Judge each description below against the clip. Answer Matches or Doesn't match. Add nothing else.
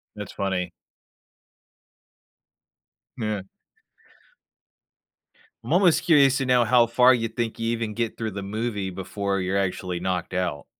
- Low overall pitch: Matches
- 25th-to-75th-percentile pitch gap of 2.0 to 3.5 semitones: Doesn't match